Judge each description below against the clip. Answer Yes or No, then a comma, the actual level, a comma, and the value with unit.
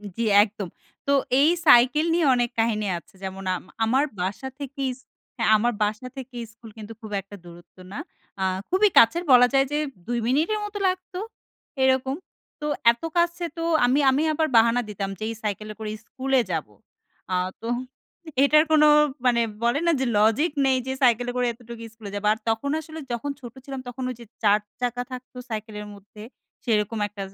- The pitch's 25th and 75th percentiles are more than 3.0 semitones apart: Yes, average, 4.2 semitones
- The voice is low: No, high, 245 Hz